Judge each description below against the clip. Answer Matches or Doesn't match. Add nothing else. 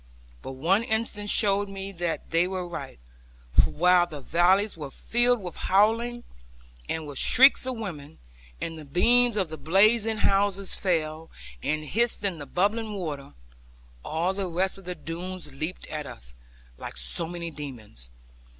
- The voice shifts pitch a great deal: Doesn't match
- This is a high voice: Doesn't match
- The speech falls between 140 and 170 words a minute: Matches